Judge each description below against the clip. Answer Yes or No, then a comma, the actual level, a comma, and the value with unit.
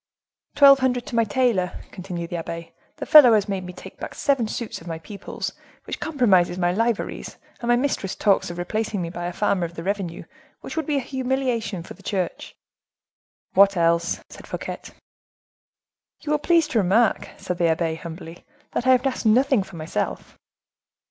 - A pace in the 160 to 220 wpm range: Yes, average, 185 wpm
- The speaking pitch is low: No, high, 200 Hz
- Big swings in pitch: Yes, wide, 6.0 semitones